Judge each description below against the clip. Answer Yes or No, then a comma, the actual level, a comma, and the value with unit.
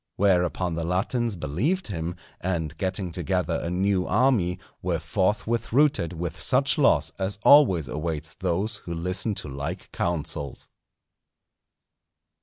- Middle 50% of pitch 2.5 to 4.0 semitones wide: Yes, average, 3.7 semitones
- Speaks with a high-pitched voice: No, very low, 90 Hz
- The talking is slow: Yes, slow, 125 wpm